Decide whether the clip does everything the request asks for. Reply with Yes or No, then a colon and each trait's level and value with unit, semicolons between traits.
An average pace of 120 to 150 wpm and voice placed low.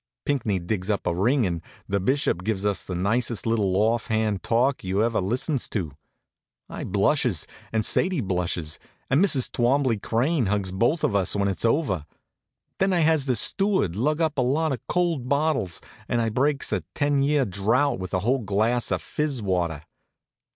No: average, 180 wpm; low, 115 Hz